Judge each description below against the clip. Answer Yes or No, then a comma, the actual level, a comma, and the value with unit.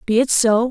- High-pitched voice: Yes, high, 235 Hz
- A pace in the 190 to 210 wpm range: No, fast, 255 wpm